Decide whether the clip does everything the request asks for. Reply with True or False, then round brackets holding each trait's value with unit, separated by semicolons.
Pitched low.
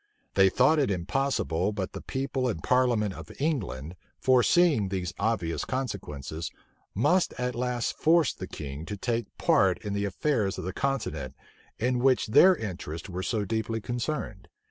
True (110 Hz)